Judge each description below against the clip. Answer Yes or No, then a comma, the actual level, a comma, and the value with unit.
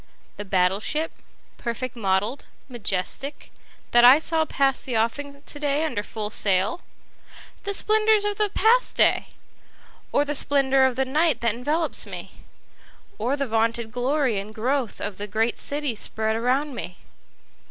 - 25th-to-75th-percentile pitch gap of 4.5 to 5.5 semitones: Yes, average, 5.0 semitones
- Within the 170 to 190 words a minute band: No, average, 145 wpm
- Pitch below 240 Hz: No, very high, 255 Hz